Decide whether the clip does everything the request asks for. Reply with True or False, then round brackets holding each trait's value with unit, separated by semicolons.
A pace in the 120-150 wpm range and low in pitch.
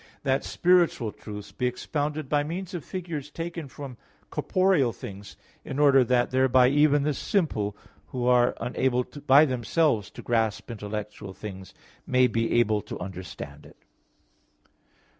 True (140 wpm; 130 Hz)